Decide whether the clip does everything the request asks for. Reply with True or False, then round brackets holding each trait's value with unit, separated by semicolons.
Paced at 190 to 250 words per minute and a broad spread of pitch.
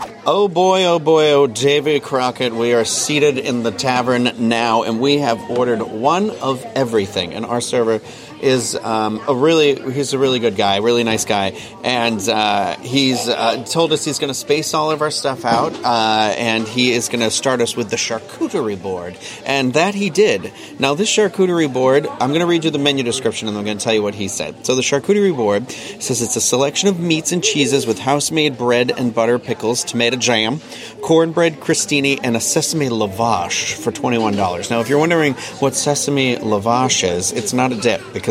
False (205 wpm; 4.3 semitones)